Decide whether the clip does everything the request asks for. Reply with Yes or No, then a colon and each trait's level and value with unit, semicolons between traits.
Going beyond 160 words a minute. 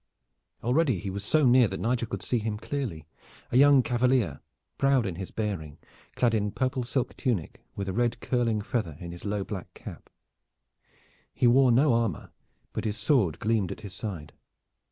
Yes: average, 175 wpm